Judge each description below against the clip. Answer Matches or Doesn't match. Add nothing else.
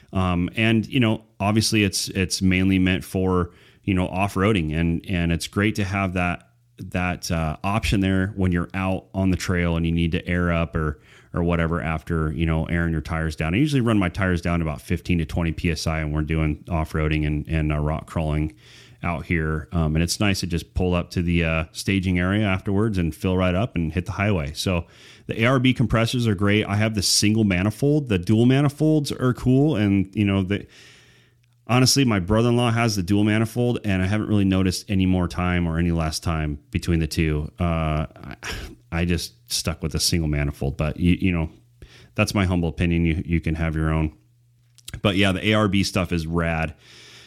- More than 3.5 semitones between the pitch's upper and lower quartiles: Matches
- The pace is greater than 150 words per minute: Matches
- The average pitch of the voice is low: Matches